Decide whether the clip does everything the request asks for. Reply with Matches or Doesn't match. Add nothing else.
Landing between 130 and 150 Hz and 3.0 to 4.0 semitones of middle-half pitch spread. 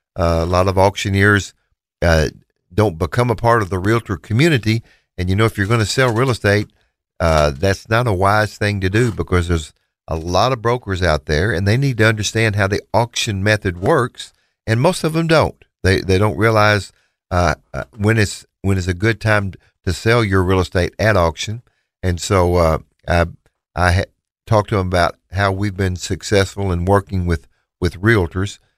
Doesn't match